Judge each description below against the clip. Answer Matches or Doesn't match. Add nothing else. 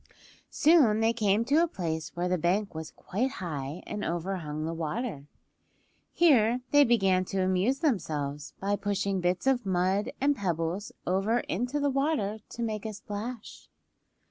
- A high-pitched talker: Matches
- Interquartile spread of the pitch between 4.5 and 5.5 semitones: Matches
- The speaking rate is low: Doesn't match